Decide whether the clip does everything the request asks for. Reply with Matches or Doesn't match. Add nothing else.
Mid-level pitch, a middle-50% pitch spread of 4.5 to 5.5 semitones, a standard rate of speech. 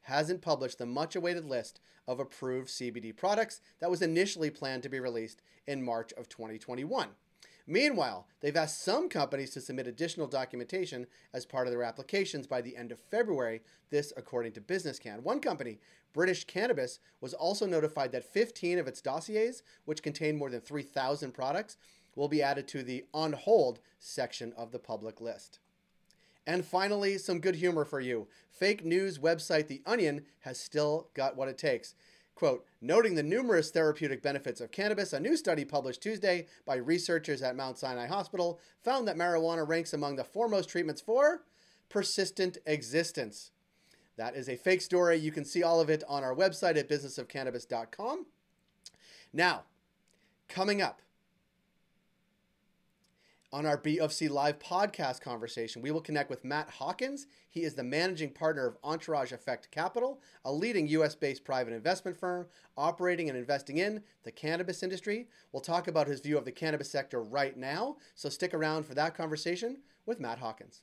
Matches